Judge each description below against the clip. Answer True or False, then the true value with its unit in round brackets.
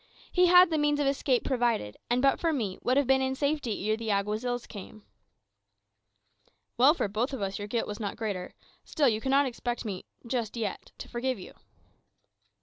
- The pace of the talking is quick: False (190 wpm)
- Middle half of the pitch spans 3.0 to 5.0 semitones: True (4.2 semitones)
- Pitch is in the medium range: False (245 Hz)